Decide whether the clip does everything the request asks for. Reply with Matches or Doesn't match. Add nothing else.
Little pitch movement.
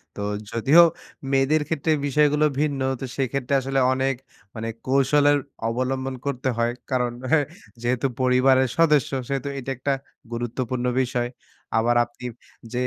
Matches